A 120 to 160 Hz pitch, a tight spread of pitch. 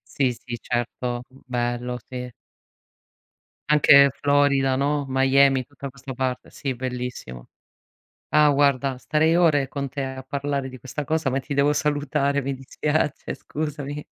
Yes: low, 135 Hz; narrow, 2.0 semitones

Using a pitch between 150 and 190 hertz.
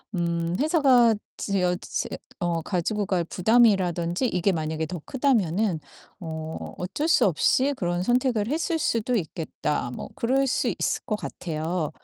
Yes: medium, 185 Hz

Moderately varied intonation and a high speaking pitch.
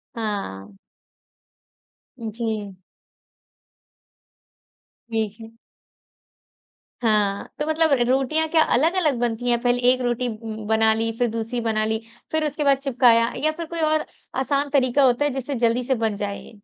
Yes: average, 4.1 semitones; high, 240 Hz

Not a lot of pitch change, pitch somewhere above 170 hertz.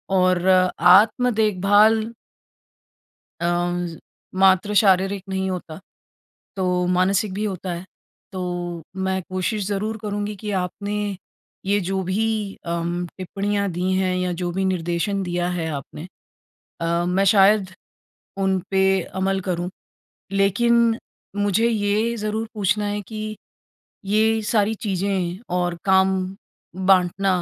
Yes: narrow, 2.3 semitones; high, 190 Hz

